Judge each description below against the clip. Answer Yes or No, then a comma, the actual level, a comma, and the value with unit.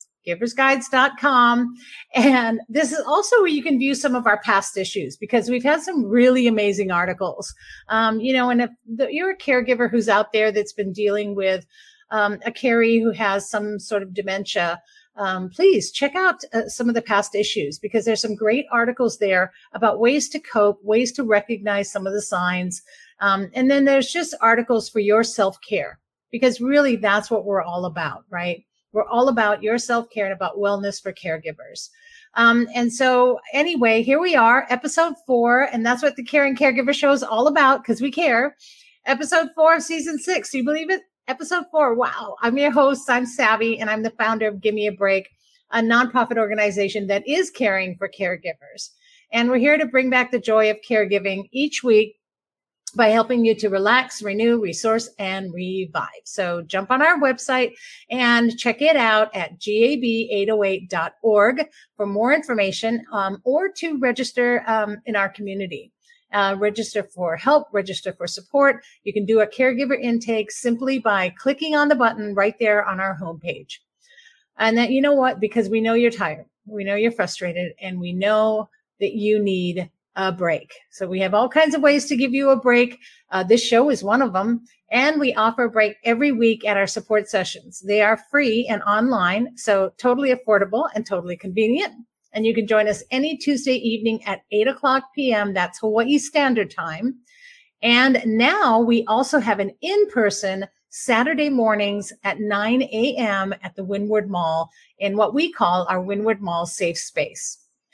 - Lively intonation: No, average, 4.4 semitones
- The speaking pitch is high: Yes, high, 225 Hz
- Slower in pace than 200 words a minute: Yes, average, 180 wpm